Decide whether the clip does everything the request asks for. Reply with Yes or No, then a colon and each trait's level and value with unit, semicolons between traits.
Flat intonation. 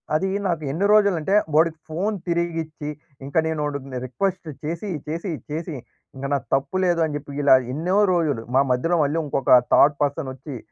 No: average, 3.4 semitones